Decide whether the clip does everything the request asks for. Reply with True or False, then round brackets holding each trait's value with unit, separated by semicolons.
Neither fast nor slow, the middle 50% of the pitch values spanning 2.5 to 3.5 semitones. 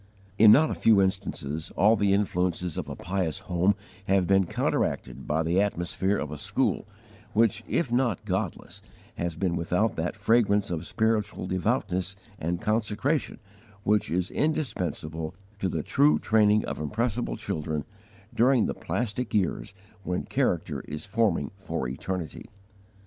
False (145 wpm; 4.0 semitones)